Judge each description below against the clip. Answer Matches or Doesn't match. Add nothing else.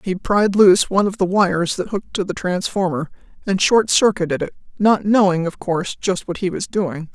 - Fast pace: Matches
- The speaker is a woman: Matches